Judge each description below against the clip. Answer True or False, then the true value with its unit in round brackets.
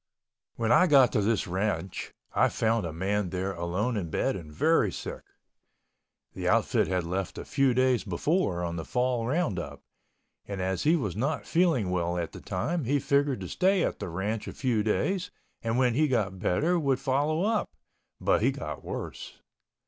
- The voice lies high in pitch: False (110 Hz)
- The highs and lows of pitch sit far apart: True (7.2 semitones)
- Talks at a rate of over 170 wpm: True (185 wpm)